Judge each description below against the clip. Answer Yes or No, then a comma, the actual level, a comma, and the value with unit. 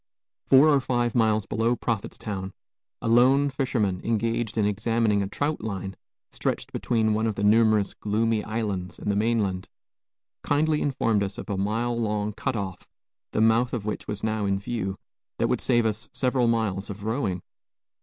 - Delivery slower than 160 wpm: No, average, 170 wpm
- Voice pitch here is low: Yes, low, 110 Hz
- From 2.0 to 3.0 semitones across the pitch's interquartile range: Yes, narrow, 2.6 semitones